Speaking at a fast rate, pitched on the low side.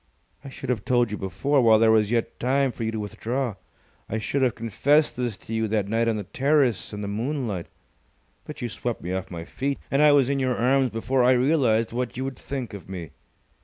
Yes: fast, 230 wpm; low, 120 Hz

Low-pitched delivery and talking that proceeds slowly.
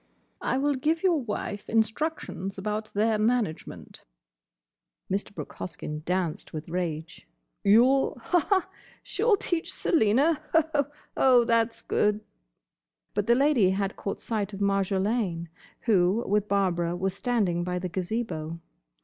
No: high, 210 Hz; slow, 115 wpm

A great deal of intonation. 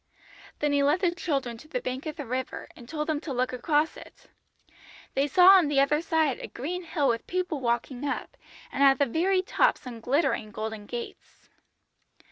No: average, 4.3 semitones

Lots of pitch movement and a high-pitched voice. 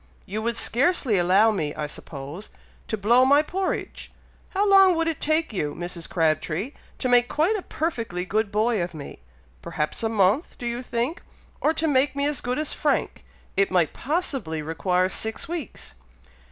Yes: wide, 8.4 semitones; high, 230 Hz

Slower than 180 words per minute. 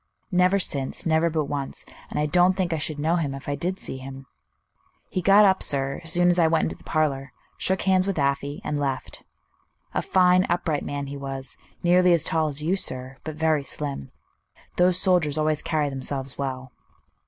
No: average, 200 wpm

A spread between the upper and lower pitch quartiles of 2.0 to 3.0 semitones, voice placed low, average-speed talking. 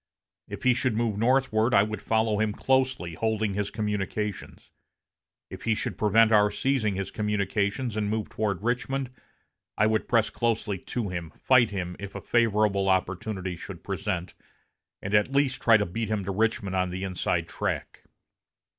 Yes: narrow, 2.6 semitones; low, 105 Hz; average, 165 wpm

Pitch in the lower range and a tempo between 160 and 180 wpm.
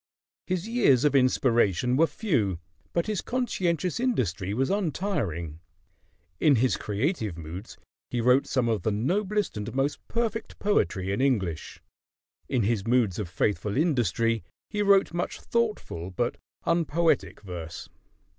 No: low, 125 Hz; slow, 135 wpm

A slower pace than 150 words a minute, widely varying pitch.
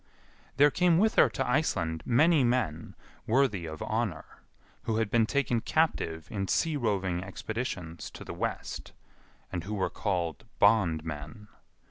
Yes: average, 140 wpm; wide, 7.0 semitones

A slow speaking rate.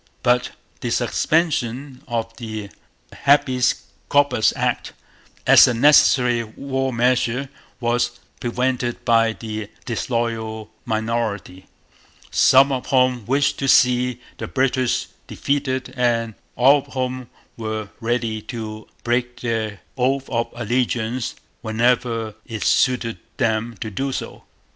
Yes: slow, 115 wpm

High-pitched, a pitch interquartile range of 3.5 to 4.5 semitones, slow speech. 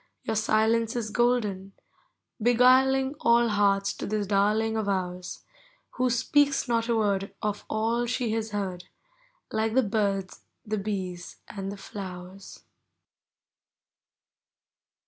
No: high, 215 Hz; average, 3.0 semitones; slow, 125 wpm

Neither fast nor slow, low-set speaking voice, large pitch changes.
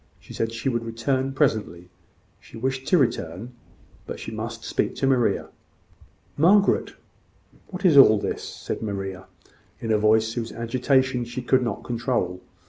No: average, 150 wpm; low, 115 Hz; average, 3.1 semitones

